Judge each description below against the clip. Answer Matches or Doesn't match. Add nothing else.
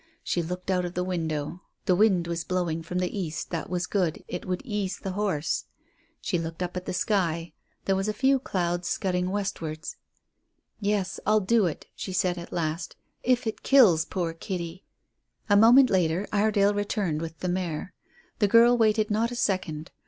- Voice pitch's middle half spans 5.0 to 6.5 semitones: Doesn't match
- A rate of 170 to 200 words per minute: Matches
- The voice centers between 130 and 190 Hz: Matches